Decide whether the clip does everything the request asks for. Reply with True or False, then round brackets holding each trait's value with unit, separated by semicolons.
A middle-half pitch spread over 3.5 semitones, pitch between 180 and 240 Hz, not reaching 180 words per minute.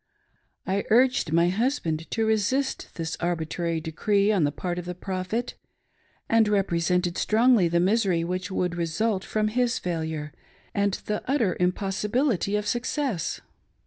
True (4.3 semitones; 190 Hz; 140 wpm)